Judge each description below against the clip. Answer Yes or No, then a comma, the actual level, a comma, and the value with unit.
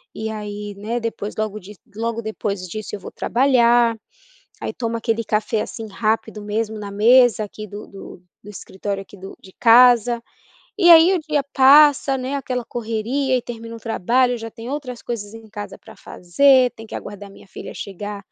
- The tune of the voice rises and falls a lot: No, average, 3.0 semitones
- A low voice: No, high, 225 Hz